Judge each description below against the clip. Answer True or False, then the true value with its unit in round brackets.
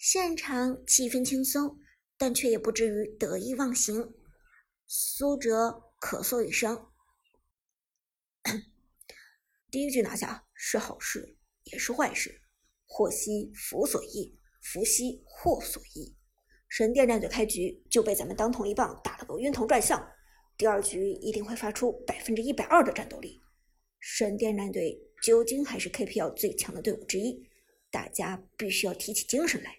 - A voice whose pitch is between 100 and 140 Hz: False (230 Hz)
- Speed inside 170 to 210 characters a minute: False (225 characters per minute)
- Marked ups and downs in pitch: False (4.1 semitones)